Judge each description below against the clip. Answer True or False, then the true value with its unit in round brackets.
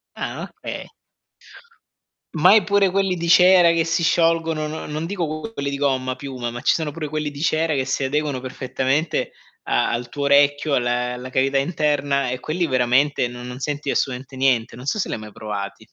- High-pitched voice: False (140 Hz)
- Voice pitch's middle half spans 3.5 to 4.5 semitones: True (3.9 semitones)